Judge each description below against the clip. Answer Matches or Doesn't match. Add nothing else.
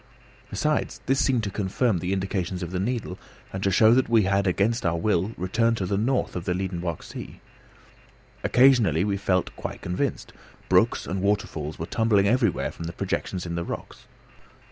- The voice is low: Matches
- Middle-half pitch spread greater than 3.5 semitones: Matches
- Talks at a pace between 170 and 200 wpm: Matches